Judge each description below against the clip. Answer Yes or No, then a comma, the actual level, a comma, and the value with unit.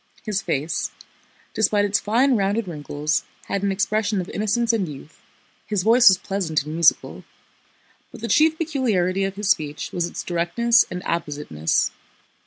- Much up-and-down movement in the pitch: No, average, 4.7 semitones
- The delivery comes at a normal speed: Yes, average, 155 wpm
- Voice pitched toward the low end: No, high, 195 Hz